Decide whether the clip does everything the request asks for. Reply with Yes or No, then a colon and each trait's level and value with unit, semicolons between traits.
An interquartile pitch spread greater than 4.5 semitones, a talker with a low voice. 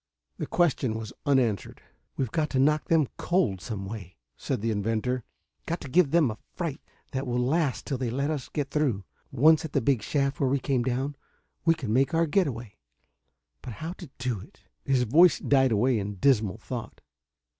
Yes: average, 4.9 semitones; low, 130 Hz